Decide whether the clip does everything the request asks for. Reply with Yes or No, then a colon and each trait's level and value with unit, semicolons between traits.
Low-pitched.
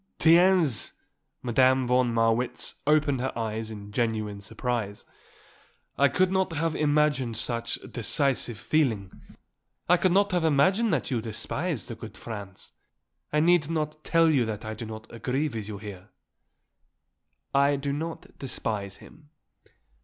Yes: low, 130 Hz